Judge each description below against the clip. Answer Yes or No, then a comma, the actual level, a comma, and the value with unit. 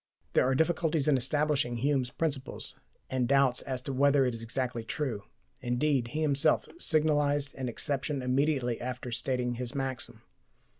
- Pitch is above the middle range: No, low, 135 Hz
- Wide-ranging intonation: No, average, 2.8 semitones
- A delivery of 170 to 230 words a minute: No, average, 150 wpm